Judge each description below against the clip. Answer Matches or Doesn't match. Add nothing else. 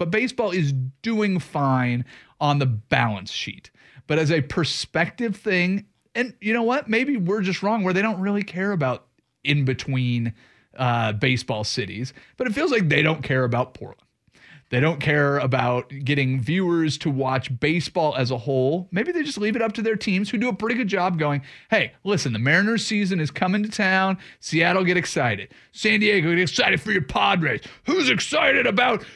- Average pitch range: Doesn't match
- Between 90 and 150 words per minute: Doesn't match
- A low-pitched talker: Doesn't match